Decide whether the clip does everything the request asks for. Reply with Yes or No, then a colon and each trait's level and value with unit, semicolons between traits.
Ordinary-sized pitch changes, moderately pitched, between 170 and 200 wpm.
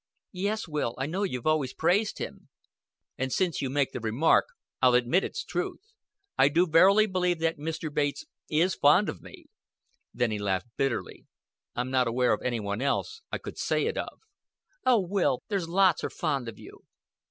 No: wide, 6.5 semitones; medium, 155 Hz; average, 185 wpm